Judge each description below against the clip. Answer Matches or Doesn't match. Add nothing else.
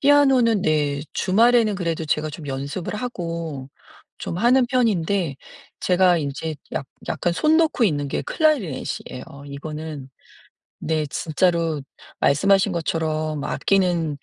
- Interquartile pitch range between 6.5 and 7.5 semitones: Doesn't match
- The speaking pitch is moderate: Matches